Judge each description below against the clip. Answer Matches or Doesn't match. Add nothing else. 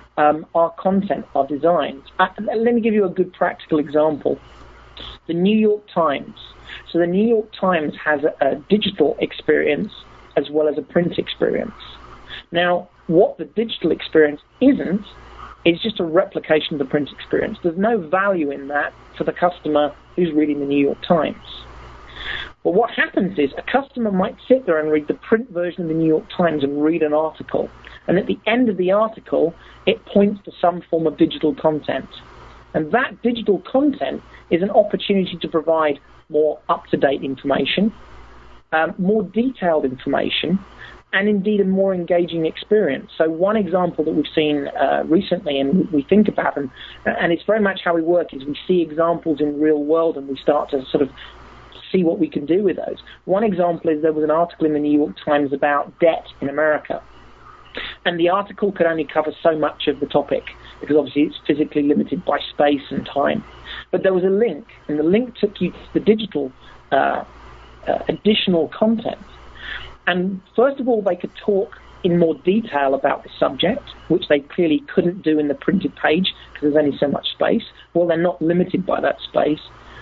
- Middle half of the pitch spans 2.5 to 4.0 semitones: Doesn't match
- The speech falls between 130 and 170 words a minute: Doesn't match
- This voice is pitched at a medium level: Matches